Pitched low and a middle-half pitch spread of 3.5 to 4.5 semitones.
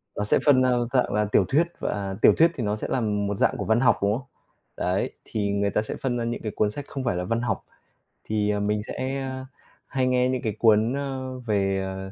Yes: low, 110 Hz; average, 3.9 semitones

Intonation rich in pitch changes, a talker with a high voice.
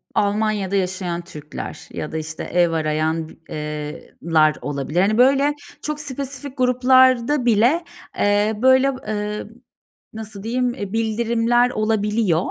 Yes: wide, 6.6 semitones; high, 215 Hz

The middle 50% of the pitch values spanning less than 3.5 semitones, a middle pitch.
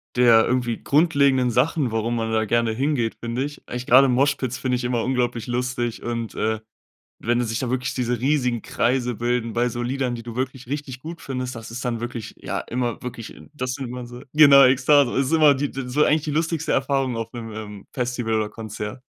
No: narrow, 2.4 semitones; low, 125 Hz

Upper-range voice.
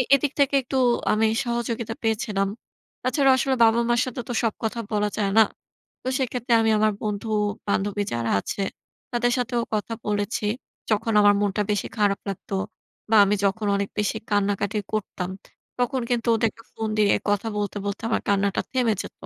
Yes: high, 215 Hz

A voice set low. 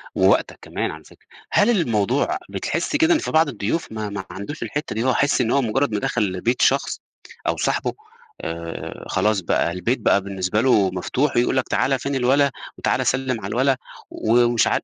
Yes: low, 120 Hz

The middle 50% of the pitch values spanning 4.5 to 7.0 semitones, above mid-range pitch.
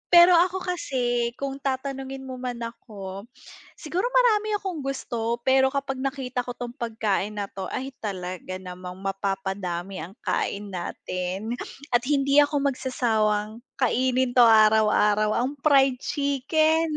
Yes: average, 4.9 semitones; high, 245 Hz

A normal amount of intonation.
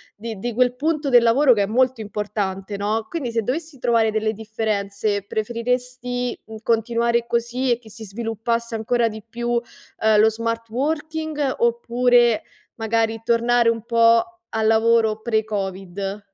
No: narrow, 1.9 semitones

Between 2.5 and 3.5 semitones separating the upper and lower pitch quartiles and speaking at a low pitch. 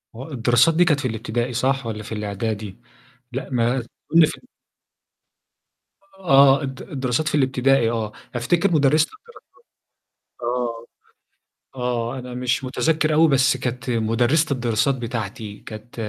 Yes: average, 3.0 semitones; low, 125 Hz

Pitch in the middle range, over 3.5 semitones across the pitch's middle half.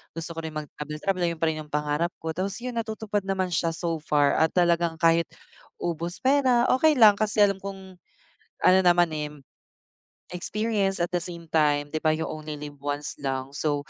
Yes: medium, 170 Hz; average, 4.1 semitones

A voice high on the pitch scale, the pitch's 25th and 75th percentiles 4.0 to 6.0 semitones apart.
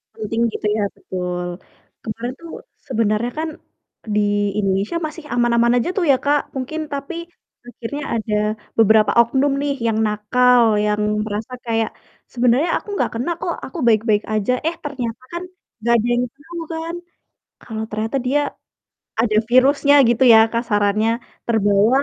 Yes: high, 235 Hz; average, 4.3 semitones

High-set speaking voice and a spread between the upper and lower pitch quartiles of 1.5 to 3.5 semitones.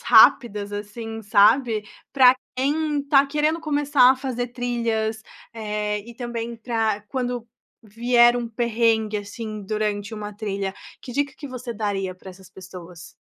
Yes: high, 230 Hz; average, 3.0 semitones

